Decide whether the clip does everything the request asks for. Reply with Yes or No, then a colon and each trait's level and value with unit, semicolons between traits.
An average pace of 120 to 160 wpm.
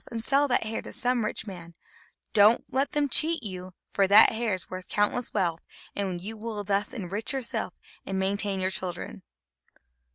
No: average, 185 wpm